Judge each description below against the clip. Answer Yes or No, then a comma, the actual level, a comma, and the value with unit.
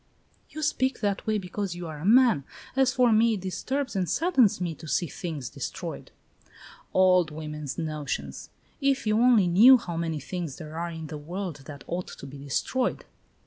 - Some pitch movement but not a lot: No, wide, 6.5 semitones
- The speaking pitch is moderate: Yes, medium, 180 Hz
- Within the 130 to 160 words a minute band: No, average, 185 wpm